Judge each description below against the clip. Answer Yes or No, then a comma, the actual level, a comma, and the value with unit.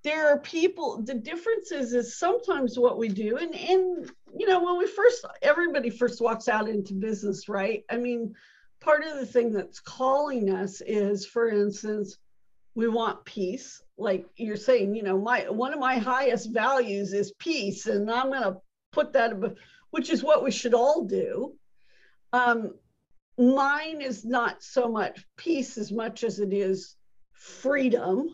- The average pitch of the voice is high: Yes, high, 245 Hz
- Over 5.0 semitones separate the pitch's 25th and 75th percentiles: Yes, wide, 5.6 semitones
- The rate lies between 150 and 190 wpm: Yes, average, 165 wpm